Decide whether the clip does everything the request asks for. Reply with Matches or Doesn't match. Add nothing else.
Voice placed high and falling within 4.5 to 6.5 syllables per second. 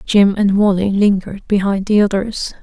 Matches